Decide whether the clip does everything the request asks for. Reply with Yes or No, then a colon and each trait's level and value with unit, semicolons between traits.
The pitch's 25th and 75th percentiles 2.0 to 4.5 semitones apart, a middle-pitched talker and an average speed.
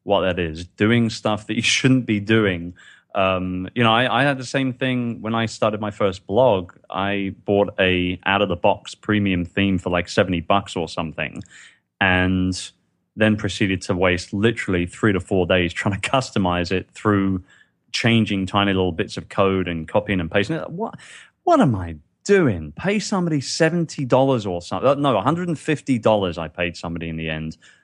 No: average, 4.0 semitones; low, 100 Hz; average, 190 wpm